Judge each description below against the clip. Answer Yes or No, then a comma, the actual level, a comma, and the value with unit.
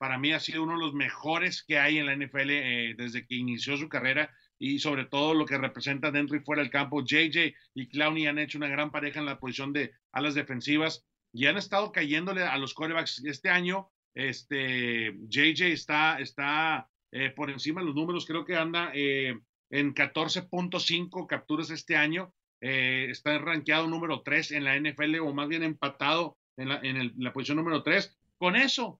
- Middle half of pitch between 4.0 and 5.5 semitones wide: No, average, 2.9 semitones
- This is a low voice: No, medium, 150 Hz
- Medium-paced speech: No, fast, 200 wpm